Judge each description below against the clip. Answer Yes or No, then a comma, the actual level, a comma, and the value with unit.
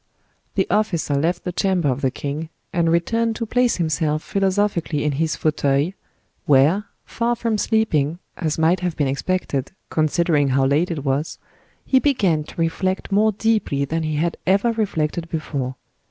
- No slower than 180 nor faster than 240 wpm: No, average, 160 wpm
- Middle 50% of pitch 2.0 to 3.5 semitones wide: No, average, 4.9 semitones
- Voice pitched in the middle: Yes, medium, 165 Hz